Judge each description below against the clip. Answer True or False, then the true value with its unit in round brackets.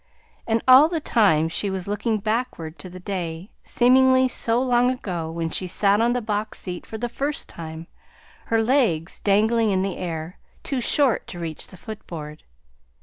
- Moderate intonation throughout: False (5.8 semitones)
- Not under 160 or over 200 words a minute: True (175 wpm)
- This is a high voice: True (210 Hz)